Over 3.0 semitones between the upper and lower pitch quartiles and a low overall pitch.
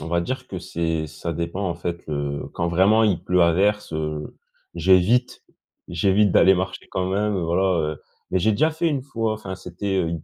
Yes: average, 3.6 semitones; very low, 95 Hz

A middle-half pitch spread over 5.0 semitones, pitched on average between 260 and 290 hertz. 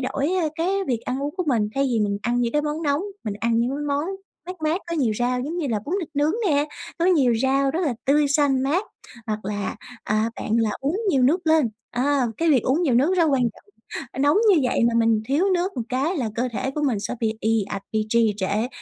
No: average, 4.4 semitones; very high, 270 Hz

